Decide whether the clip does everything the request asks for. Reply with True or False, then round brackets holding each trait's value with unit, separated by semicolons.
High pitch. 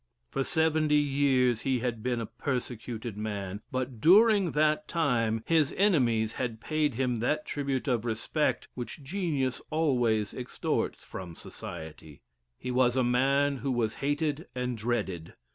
False (130 Hz)